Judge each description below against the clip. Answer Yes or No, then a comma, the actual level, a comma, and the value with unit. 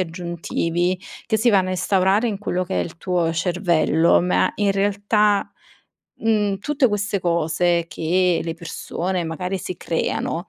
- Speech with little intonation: No, average, 3.0 semitones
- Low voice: No, medium, 185 Hz